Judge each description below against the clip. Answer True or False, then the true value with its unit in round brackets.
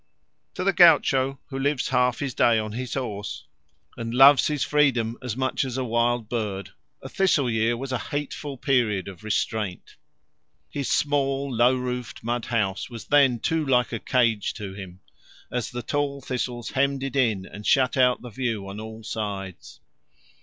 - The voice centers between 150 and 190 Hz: False (125 Hz)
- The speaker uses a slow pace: False (175 wpm)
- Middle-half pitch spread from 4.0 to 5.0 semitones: False (3.5 semitones)